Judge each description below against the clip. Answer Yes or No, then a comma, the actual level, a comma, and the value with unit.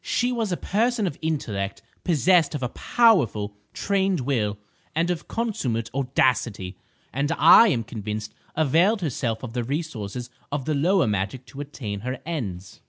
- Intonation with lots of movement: Yes, wide, 7.7 semitones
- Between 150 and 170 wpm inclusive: Yes, average, 155 wpm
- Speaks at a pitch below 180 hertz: Yes, medium, 140 Hz